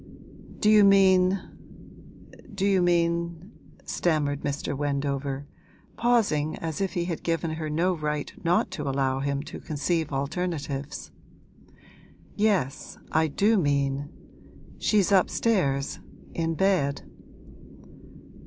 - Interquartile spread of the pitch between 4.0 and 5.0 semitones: Yes, average, 4.5 semitones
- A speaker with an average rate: No, slow, 110 wpm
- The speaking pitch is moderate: Yes, medium, 160 Hz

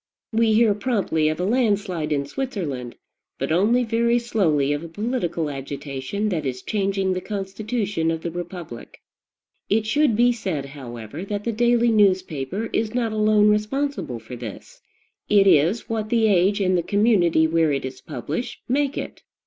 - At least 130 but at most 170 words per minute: Yes, average, 165 wpm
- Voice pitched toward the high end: Yes, high, 195 Hz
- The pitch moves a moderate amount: No, wide, 6.2 semitones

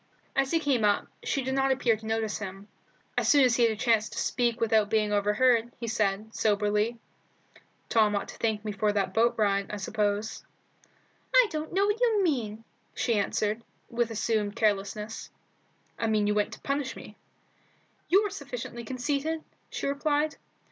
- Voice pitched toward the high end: Yes, high, 225 Hz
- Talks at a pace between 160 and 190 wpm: Yes, average, 175 wpm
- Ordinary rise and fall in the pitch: Yes, average, 4.1 semitones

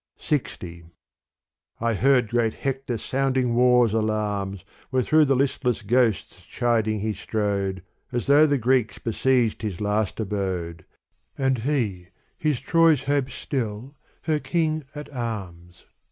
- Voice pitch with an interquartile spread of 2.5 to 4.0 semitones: No, average, 4.5 semitones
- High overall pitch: No, low, 120 Hz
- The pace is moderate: No, slow, 130 wpm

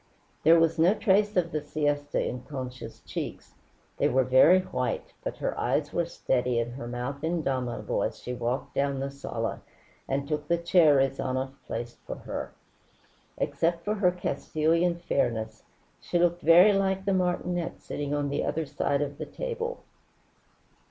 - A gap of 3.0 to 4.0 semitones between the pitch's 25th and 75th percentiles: No, average, 4.7 semitones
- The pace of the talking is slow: No, average, 160 wpm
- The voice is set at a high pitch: No, medium, 150 Hz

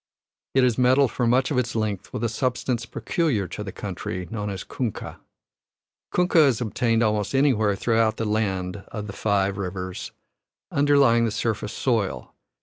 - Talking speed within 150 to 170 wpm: Yes, average, 160 wpm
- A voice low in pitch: Yes, low, 115 Hz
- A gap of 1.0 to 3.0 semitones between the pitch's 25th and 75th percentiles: No, average, 3.6 semitones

